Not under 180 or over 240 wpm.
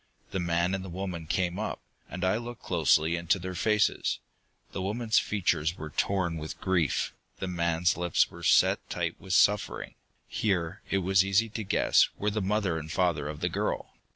Yes: average, 185 wpm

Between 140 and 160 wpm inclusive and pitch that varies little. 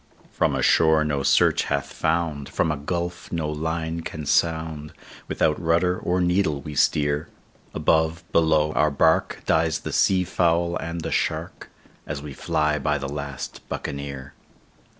Yes: average, 150 wpm; narrow, 2.3 semitones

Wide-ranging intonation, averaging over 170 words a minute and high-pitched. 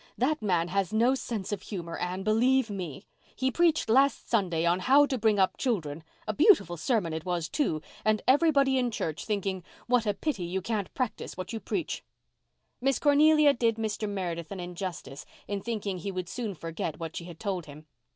Yes: wide, 6.1 semitones; average, 190 wpm; high, 205 Hz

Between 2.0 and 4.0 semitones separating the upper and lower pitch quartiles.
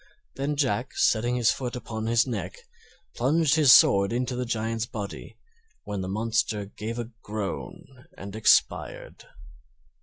Yes: average, 3.0 semitones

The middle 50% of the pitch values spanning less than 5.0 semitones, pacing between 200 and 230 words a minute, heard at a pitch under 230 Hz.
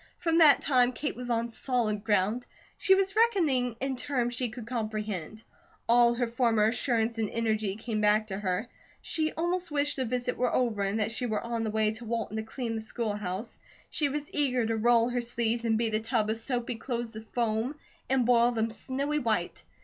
No: narrow, 2.4 semitones; fast, 205 wpm; high, 235 Hz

